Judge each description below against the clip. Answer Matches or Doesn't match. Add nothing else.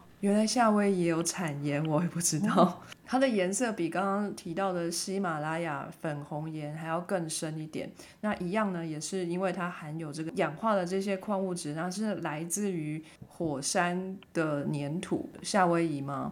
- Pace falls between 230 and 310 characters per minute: Matches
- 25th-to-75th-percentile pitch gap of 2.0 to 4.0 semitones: Matches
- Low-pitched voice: Doesn't match